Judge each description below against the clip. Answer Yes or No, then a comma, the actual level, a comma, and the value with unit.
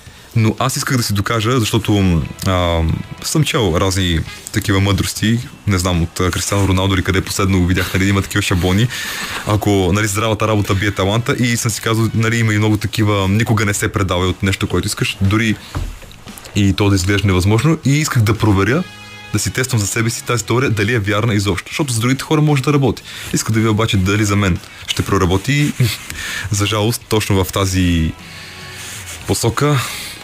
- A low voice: Yes, low, 105 Hz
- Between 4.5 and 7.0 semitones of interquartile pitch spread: No, average, 3.1 semitones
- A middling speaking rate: No, fast, 185 wpm